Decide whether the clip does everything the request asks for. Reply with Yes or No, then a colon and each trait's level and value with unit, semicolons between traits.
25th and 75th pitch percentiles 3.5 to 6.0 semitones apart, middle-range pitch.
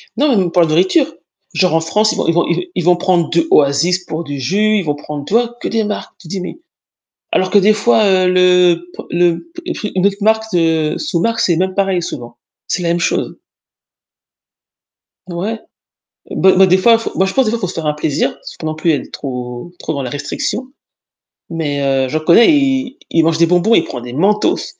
Yes: average, 4.7 semitones; medium, 180 Hz